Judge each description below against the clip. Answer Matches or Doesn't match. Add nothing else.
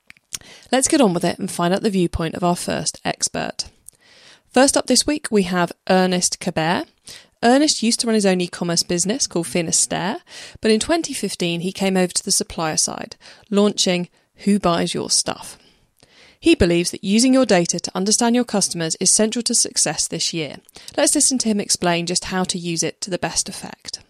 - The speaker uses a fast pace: Doesn't match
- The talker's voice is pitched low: Doesn't match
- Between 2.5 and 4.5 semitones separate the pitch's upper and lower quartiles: Doesn't match